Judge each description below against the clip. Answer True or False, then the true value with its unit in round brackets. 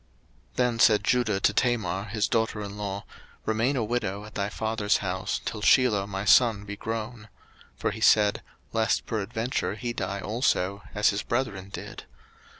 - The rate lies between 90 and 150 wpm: False (165 wpm)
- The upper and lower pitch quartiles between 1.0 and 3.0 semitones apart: True (2.4 semitones)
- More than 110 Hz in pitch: False (105 Hz)